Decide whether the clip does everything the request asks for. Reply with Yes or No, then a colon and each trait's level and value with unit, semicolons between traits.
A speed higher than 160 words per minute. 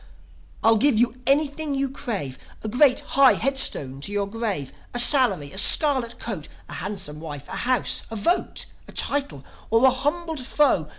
Yes: average, 170 wpm